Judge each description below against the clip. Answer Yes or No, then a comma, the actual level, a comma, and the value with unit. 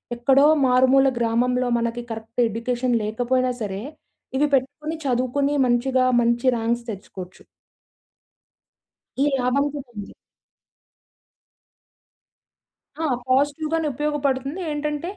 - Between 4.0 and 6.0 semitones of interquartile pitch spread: No, average, 3.0 semitones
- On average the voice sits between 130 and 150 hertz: No, very high, 255 Hz